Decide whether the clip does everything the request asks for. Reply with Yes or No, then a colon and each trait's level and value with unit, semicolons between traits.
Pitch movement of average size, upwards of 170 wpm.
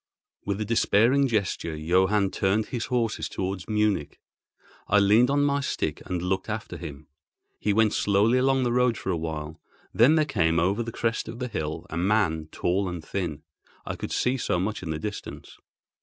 Yes: average, 5.0 semitones; average, 185 wpm